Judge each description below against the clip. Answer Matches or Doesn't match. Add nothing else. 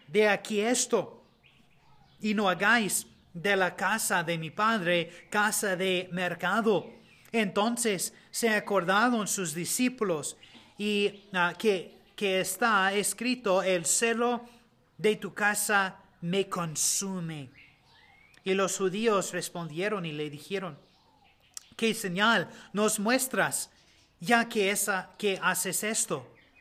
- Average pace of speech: Doesn't match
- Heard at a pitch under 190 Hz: Doesn't match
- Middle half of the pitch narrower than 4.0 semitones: Matches